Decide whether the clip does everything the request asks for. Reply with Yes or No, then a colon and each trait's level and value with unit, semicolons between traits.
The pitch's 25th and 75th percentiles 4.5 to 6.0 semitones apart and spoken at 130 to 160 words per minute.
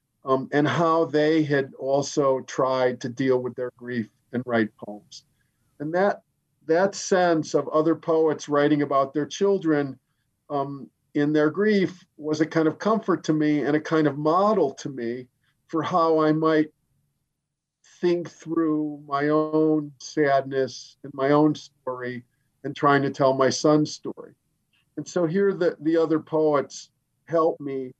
No: average, 2.9 semitones; average, 155 wpm